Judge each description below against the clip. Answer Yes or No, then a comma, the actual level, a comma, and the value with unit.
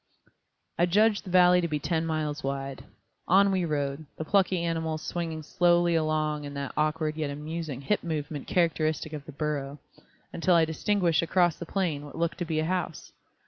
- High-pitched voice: No, medium, 160 Hz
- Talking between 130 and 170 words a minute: No, average, 185 wpm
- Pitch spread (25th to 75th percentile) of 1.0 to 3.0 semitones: Yes, narrow, 2.4 semitones